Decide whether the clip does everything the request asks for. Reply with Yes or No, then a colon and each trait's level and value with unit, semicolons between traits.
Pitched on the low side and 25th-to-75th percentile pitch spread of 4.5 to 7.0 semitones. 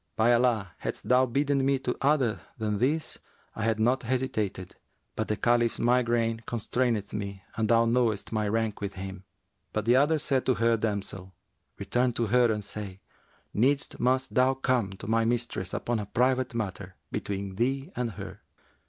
No: low, 115 Hz; average, 3.4 semitones